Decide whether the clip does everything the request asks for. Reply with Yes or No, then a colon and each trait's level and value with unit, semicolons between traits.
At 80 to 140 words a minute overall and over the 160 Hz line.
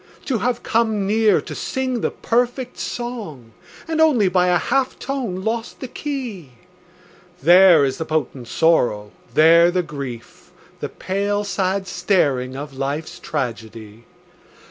Yes: slow, 135 wpm; medium, 185 Hz